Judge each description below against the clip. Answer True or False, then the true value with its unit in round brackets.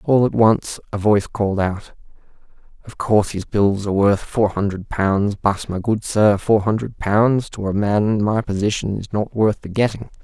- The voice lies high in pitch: False (105 Hz)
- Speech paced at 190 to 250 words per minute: True (200 wpm)